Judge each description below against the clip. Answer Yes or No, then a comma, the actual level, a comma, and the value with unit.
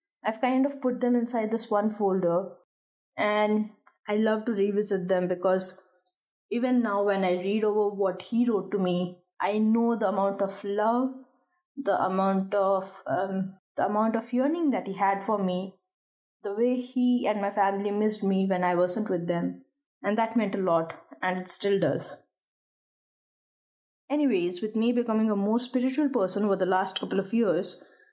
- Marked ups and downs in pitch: No, average, 3.5 semitones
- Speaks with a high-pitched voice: Yes, high, 205 Hz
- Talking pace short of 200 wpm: Yes, average, 175 wpm